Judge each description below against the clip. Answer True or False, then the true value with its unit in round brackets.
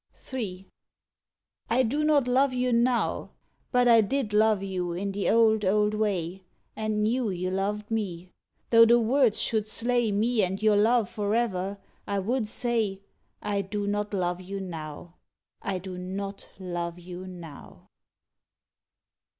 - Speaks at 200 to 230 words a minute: False (145 wpm)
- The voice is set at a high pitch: True (205 Hz)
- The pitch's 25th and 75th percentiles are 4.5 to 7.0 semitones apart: False (3.5 semitones)